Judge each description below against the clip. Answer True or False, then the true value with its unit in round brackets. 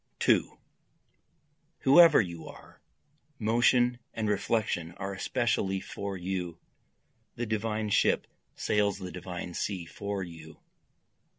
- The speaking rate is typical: False (105 wpm)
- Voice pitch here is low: True (100 Hz)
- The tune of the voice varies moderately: True (3.8 semitones)